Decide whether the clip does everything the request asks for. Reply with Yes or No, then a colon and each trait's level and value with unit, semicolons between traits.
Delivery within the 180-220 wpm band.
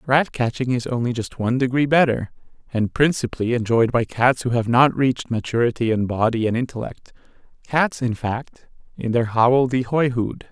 No: average, 170 wpm